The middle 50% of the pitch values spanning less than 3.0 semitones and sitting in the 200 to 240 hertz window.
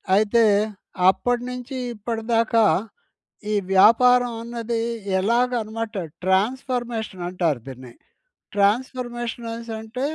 Yes: narrow, 2.4 semitones; high, 230 Hz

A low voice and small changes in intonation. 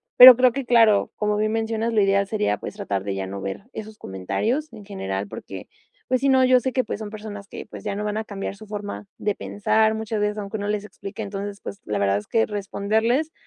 No: high, 210 Hz; narrow, 2.0 semitones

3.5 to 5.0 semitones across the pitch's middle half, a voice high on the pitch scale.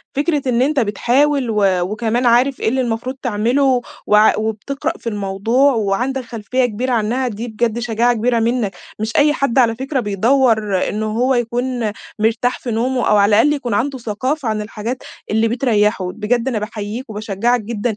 No: average, 3.1 semitones; high, 235 Hz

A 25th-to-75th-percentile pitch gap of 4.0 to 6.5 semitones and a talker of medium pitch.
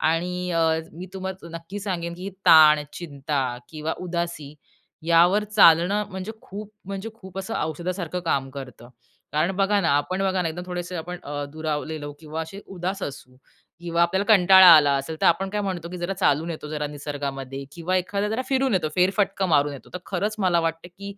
No: average, 3.6 semitones; medium, 175 Hz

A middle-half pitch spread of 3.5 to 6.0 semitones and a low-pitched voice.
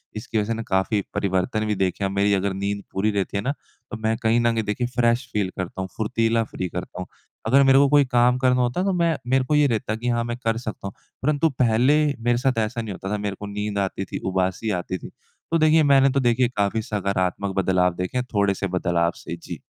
Yes: average, 3.9 semitones; low, 110 Hz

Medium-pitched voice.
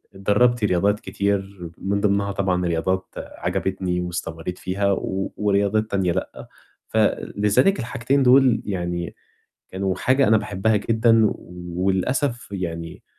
No: low, 100 Hz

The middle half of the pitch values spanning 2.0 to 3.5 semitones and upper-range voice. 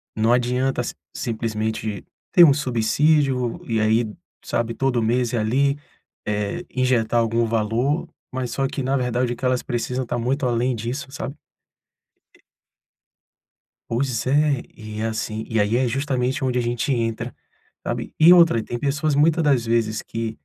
No: average, 3.0 semitones; low, 120 Hz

